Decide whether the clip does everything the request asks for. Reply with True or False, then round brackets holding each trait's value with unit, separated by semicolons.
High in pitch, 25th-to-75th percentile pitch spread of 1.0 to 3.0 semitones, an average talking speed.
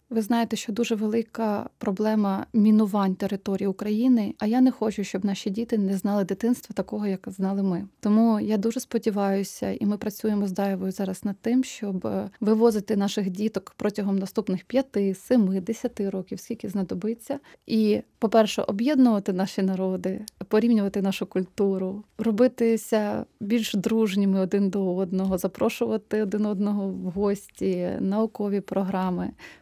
True (210 Hz; 2.4 semitones; 140 wpm)